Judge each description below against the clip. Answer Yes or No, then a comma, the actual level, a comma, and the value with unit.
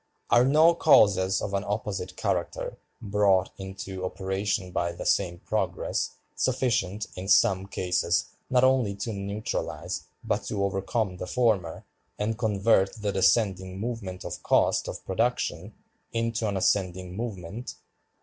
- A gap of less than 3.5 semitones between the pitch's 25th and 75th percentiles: Yes, average, 3.1 semitones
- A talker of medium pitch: No, low, 100 Hz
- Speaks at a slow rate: Yes, slow, 130 wpm